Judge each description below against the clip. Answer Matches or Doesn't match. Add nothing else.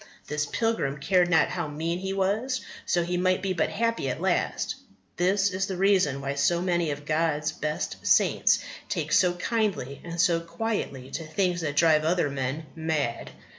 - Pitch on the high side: Doesn't match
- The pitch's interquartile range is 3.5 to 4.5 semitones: Matches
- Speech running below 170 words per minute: Doesn't match